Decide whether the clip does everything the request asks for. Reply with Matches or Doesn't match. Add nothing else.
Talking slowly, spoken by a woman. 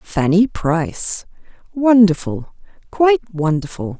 Matches